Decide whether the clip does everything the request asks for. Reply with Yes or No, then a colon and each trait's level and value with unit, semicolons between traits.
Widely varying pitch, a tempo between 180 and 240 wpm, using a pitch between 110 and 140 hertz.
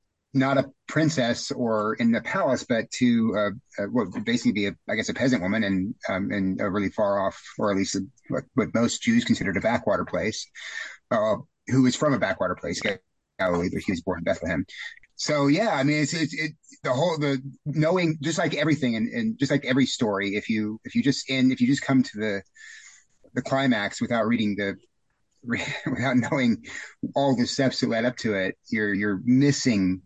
Yes: wide, 6.2 semitones; fast, 205 wpm; low, 135 Hz